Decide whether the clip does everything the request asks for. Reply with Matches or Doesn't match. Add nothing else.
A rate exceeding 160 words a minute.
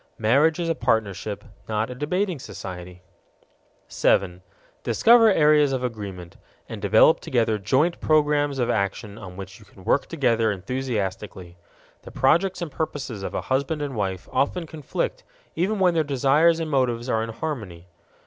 Doesn't match